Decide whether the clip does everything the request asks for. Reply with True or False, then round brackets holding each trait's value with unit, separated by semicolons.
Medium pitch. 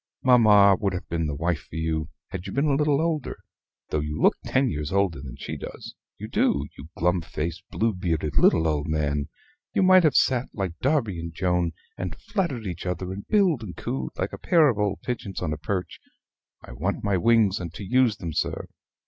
False (95 Hz)